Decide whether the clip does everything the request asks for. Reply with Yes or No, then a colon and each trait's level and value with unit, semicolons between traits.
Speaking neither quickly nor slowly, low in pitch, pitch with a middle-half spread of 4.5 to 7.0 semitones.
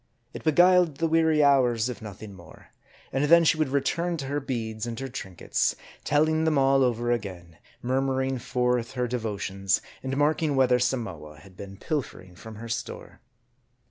Yes: average, 170 wpm; low, 125 Hz; average, 4.9 semitones